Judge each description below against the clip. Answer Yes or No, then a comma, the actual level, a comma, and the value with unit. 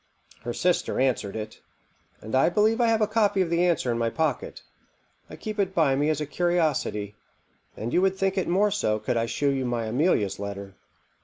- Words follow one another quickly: Yes, fast, 210 wpm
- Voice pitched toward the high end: No, medium, 150 Hz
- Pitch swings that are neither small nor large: No, wide, 8.5 semitones